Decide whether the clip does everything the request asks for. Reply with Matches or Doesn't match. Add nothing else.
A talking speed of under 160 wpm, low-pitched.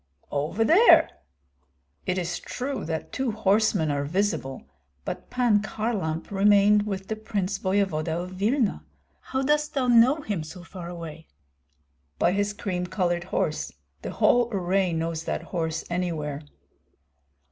Doesn't match